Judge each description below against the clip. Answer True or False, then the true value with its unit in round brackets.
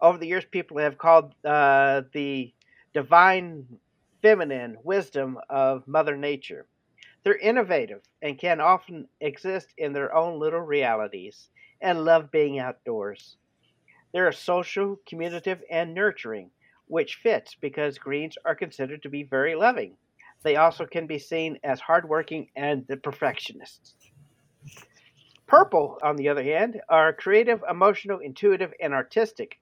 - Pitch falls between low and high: True (155 Hz)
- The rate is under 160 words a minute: True (135 wpm)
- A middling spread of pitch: True (4.3 semitones)